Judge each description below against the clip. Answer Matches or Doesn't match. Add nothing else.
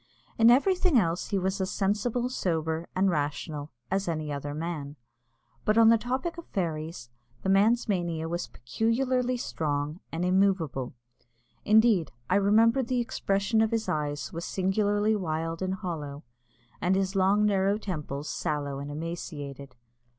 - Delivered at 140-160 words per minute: Matches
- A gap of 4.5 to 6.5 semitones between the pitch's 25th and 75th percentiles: Matches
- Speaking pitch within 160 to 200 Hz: Matches